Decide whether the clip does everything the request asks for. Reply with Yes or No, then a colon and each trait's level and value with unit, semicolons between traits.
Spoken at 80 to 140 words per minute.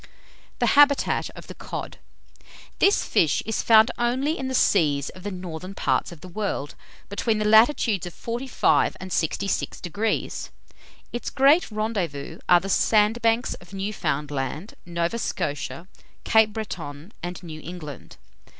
Yes: slow, 135 wpm